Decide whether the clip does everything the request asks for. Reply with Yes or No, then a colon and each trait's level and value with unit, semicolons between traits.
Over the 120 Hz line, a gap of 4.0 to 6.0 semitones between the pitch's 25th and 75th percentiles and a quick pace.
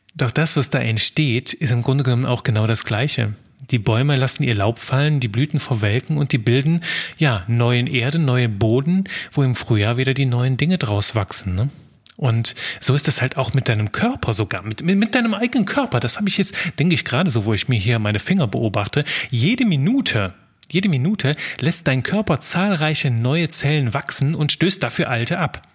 Yes: low, 135 Hz; average, 5.0 semitones; fast, 200 wpm